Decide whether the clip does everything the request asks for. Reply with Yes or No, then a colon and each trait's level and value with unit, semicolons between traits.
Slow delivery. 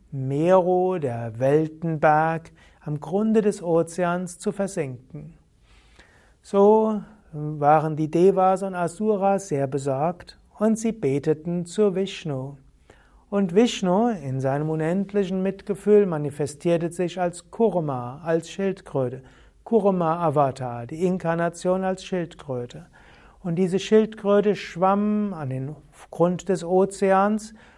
Yes: slow, 105 wpm